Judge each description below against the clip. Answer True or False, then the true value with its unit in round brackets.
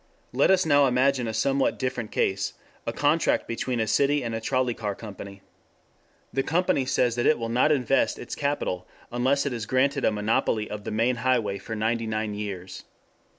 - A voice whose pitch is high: False (120 Hz)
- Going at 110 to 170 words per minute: False (190 wpm)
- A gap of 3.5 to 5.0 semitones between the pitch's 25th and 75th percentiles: True (4.0 semitones)